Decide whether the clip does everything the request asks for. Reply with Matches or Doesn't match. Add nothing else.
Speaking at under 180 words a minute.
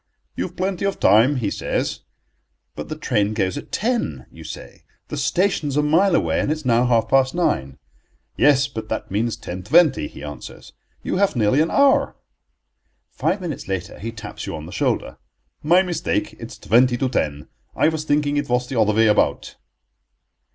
Doesn't match